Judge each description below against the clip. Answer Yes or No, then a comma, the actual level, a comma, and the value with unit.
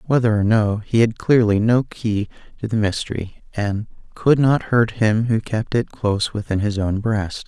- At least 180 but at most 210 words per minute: Yes, average, 195 wpm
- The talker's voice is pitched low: Yes, low, 110 Hz